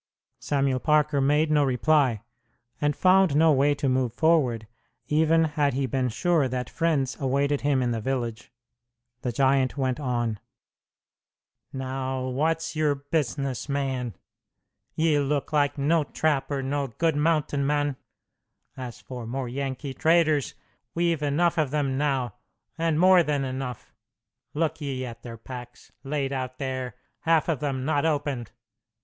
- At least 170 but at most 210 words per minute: No, average, 145 wpm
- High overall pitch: No, medium, 140 Hz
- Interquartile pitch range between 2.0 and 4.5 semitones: Yes, average, 2.8 semitones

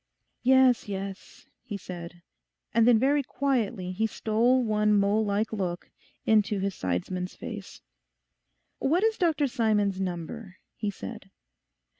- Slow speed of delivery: Yes, slow, 125 wpm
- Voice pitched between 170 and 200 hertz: No, high, 210 Hz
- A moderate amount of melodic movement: Yes, average, 4.1 semitones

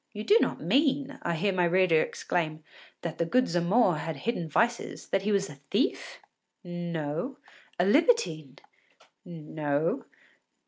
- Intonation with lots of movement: Yes, wide, 6.7 semitones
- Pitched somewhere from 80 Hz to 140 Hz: No, medium, 175 Hz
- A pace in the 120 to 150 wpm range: Yes, average, 140 wpm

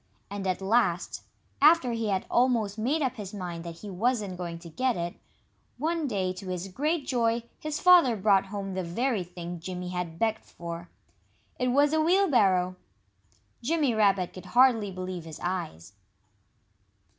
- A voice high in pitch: Yes, high, 200 Hz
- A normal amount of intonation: No, wide, 5.8 semitones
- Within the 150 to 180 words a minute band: Yes, average, 160 wpm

